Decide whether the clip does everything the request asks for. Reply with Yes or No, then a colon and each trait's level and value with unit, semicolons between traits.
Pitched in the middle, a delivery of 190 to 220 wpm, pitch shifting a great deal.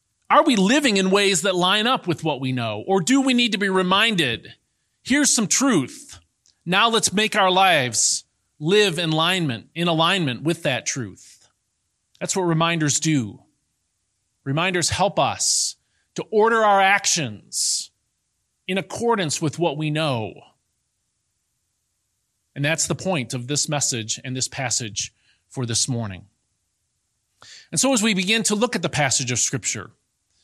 No: medium, 165 Hz; average, 150 wpm; wide, 8.0 semitones